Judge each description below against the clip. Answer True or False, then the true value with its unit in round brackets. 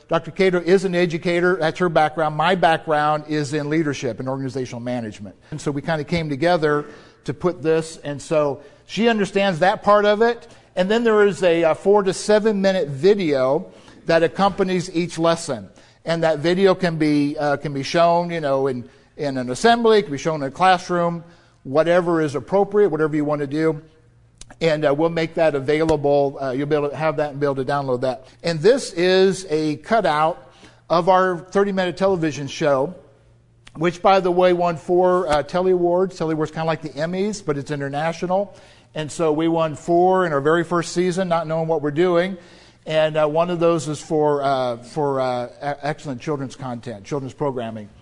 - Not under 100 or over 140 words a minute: False (195 wpm)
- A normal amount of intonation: True (3.8 semitones)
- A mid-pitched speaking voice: True (160 Hz)